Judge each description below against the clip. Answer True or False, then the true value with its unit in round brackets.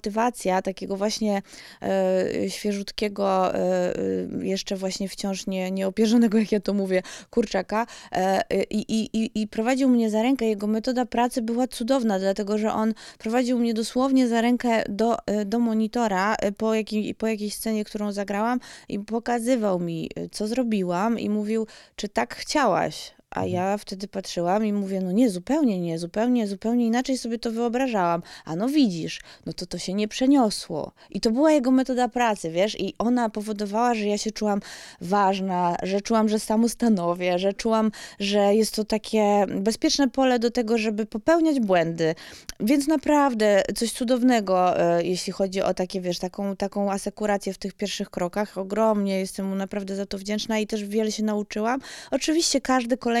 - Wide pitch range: False (3.1 semitones)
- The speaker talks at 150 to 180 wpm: True (160 wpm)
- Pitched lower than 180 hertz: False (215 Hz)